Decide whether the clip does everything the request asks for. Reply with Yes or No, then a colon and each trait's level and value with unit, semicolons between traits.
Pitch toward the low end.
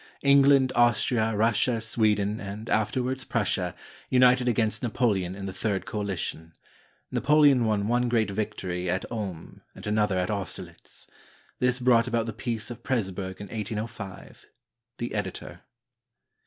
Yes: low, 110 Hz